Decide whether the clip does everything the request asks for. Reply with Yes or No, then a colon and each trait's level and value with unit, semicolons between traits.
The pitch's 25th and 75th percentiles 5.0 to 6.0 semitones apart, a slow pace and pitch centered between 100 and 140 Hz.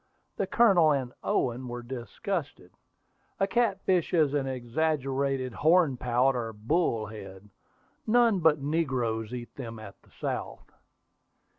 Yes: wide, 5.6 semitones; slow, 115 wpm; low, 135 Hz